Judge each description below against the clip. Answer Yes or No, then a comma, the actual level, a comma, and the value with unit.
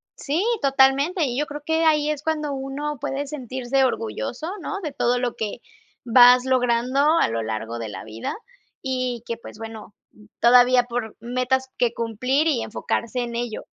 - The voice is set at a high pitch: Yes, very high, 250 Hz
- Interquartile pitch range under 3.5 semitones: Yes, average, 3.1 semitones